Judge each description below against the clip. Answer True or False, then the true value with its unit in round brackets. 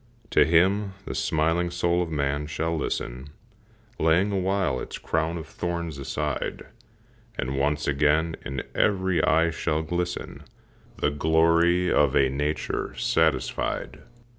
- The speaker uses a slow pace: True (125 wpm)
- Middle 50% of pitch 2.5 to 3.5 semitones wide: True (3.0 semitones)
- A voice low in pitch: True (80 Hz)